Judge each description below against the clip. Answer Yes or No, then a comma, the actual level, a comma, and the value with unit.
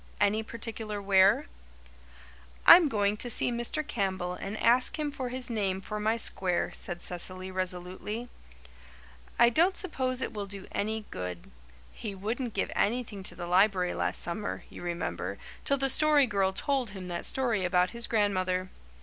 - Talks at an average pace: Yes, average, 160 wpm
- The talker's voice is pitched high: Yes, high, 205 Hz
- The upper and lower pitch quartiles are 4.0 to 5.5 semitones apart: Yes, average, 4.4 semitones